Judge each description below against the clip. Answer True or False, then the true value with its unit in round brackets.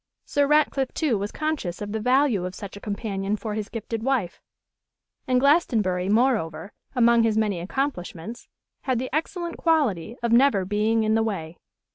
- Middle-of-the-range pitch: False (225 Hz)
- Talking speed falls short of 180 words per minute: True (165 wpm)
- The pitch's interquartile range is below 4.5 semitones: False (4.9 semitones)